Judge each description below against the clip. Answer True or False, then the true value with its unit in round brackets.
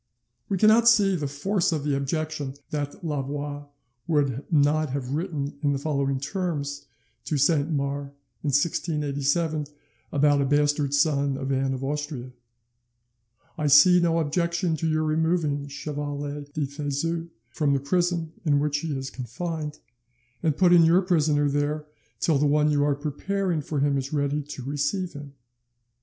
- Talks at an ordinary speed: True (155 wpm)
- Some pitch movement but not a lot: False (2.3 semitones)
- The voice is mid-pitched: True (145 Hz)